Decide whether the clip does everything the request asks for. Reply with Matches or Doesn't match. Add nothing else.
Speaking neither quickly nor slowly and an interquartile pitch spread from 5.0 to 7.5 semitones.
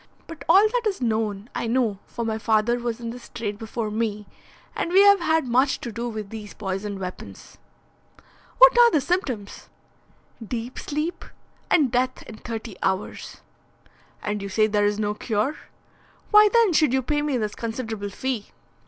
Matches